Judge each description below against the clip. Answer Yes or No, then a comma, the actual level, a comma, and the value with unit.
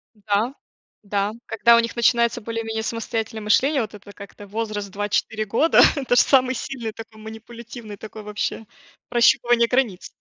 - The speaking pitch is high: Yes, high, 225 Hz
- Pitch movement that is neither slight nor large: No, narrow, 2.1 semitones